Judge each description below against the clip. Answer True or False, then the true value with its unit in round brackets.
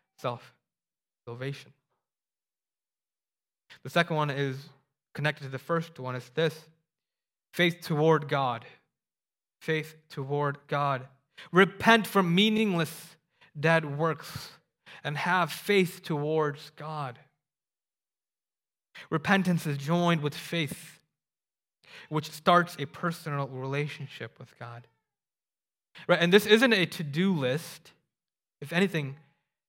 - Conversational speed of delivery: False (100 wpm)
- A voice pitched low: False (155 Hz)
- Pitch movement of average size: True (3.4 semitones)